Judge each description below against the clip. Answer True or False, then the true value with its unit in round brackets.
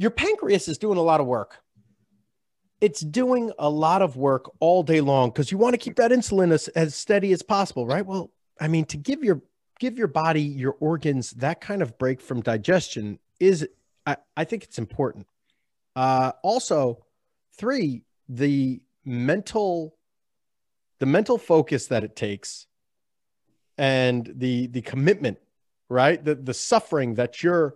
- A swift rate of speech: False (160 wpm)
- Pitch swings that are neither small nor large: False (6.9 semitones)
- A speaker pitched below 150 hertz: False (155 Hz)